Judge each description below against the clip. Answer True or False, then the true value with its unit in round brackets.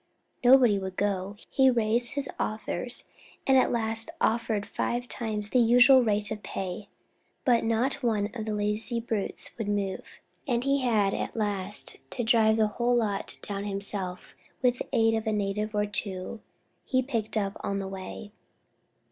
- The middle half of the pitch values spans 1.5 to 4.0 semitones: True (2.7 semitones)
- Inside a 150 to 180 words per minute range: True (165 wpm)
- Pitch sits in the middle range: False (220 Hz)